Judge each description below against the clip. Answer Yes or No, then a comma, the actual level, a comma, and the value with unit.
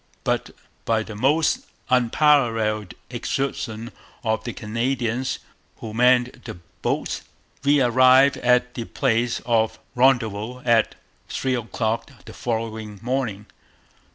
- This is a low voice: Yes, low, 120 Hz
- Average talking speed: No, slow, 110 wpm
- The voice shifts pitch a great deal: No, narrow, 2.5 semitones